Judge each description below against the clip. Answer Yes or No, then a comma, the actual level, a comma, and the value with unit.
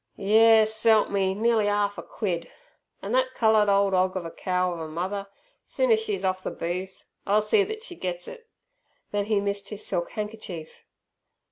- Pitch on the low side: No, high, 205 Hz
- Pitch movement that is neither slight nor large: Yes, average, 3.1 semitones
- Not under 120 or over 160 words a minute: No, average, 180 wpm